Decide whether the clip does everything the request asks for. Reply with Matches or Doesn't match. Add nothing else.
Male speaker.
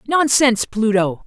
Doesn't match